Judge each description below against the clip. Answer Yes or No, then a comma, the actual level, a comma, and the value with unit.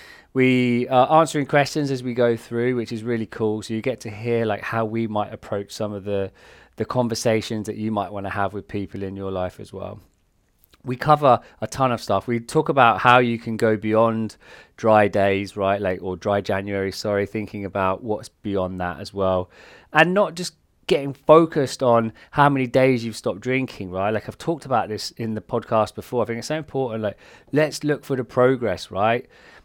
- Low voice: Yes, low, 110 Hz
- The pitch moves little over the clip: No, average, 4.0 semitones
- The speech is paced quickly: Yes, fast, 210 wpm